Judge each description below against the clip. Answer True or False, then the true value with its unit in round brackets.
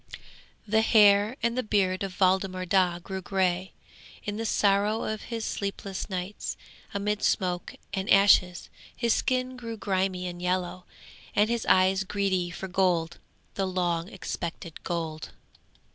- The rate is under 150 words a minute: True (140 wpm)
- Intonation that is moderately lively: False (2.3 semitones)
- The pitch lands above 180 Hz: True (190 Hz)